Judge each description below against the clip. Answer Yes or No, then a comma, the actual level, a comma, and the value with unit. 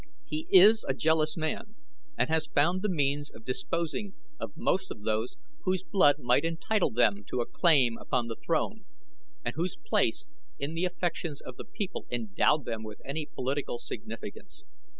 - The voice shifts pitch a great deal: Yes, wide, 6.1 semitones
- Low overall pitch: No, medium, 150 Hz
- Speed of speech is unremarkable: Yes, average, 170 wpm